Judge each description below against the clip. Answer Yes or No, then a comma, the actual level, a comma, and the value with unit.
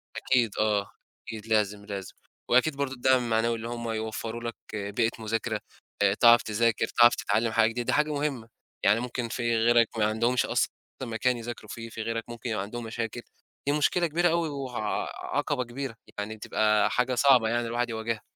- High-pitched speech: No, low, 115 Hz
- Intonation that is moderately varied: No, narrow, 1.9 semitones